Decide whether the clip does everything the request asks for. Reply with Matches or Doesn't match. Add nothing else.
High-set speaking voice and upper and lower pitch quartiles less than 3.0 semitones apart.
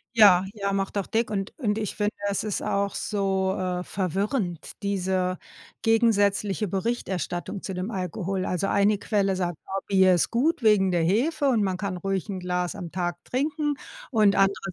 Matches